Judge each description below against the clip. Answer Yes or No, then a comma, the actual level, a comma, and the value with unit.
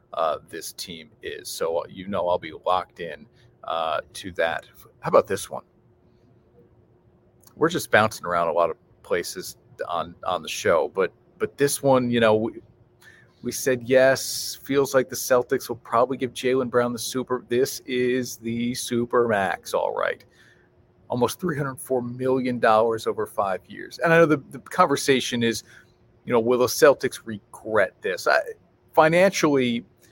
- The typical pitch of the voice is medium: No, low, 130 Hz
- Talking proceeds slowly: No, average, 165 wpm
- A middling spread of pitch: Yes, average, 4.3 semitones